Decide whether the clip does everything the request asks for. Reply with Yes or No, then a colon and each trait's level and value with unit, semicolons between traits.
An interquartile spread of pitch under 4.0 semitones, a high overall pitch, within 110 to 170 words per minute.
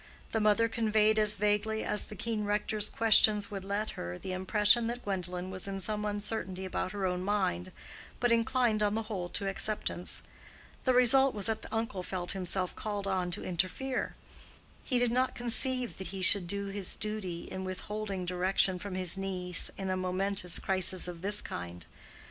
No: average, 2.7 semitones; high, 200 Hz; average, 180 wpm